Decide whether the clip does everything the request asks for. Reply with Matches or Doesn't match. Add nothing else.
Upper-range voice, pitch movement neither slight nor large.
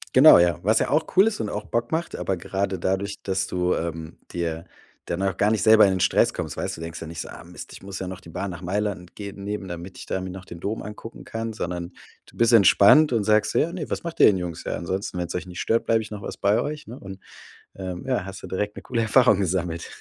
Doesn't match